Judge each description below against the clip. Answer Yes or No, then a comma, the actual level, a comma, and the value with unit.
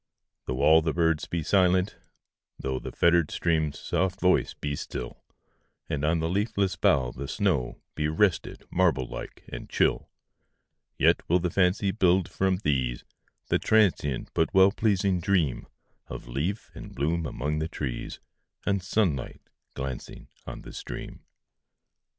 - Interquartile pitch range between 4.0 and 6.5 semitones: Yes, average, 4.7 semitones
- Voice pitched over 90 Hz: No, very low, 85 Hz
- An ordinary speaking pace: No, slow, 120 wpm